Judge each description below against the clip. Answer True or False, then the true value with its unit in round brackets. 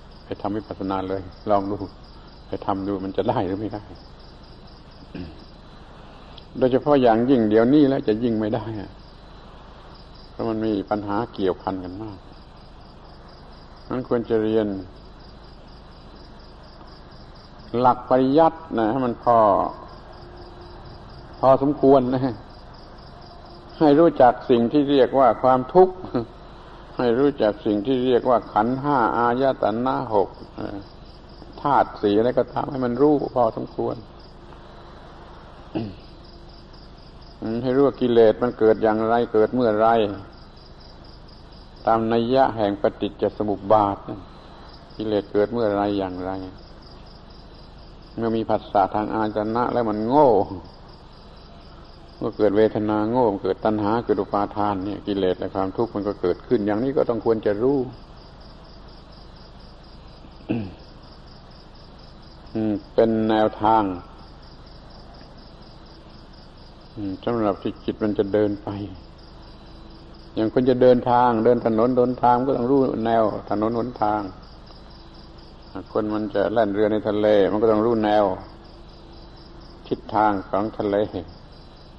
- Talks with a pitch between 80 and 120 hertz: True (105 Hz)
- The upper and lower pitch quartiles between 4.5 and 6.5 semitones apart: False (3.3 semitones)